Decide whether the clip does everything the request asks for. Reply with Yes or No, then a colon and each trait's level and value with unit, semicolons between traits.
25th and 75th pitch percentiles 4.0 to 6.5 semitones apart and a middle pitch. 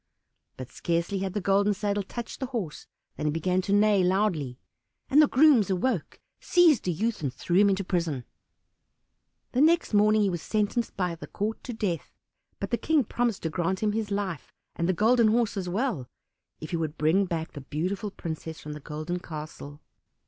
No: average, 4.6 semitones; high, 195 Hz